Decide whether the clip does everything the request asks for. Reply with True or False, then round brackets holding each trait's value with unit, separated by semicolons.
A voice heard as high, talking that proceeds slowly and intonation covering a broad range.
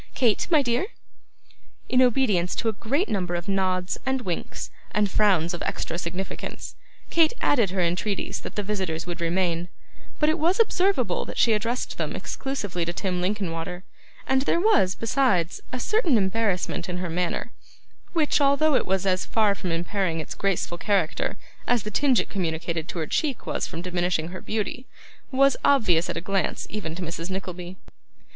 False (195 Hz; 175 wpm; 5.9 semitones)